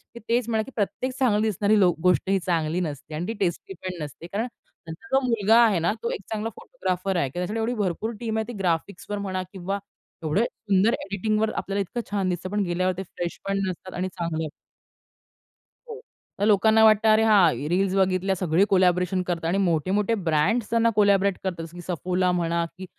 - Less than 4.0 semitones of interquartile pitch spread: Yes, average, 3.4 semitones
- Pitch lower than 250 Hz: Yes, high, 190 Hz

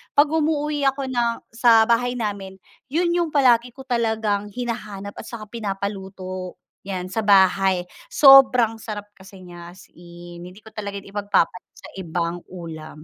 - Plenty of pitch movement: No, average, 4.5 semitones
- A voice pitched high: Yes, high, 210 Hz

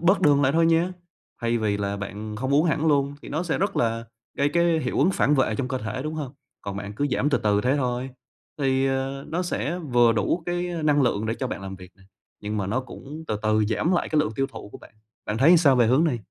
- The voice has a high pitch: No, low, 135 Hz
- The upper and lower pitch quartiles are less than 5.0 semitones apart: No, wide, 5.6 semitones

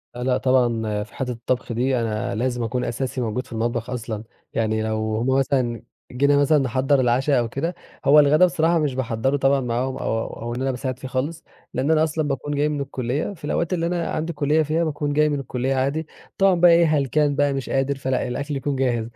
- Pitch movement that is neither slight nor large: Yes, average, 3.2 semitones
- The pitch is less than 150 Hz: Yes, low, 135 Hz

